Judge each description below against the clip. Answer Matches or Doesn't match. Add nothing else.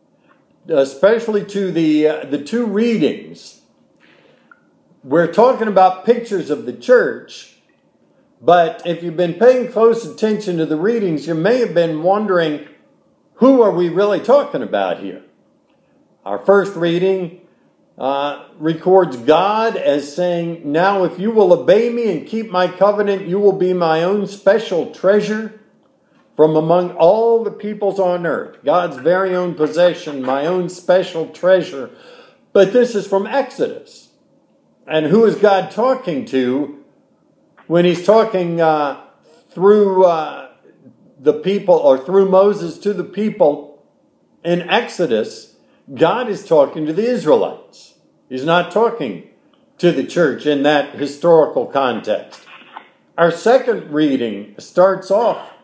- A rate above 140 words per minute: Doesn't match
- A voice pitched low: Doesn't match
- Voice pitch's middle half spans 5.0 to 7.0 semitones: Doesn't match